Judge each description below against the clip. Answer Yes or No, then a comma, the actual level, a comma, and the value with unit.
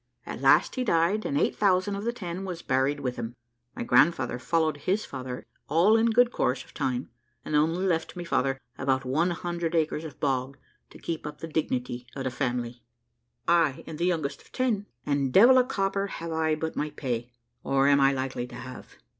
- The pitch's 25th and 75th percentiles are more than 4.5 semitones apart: Yes, average, 5.2 semitones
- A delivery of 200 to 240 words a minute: Yes, fast, 205 wpm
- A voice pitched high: No, medium, 155 Hz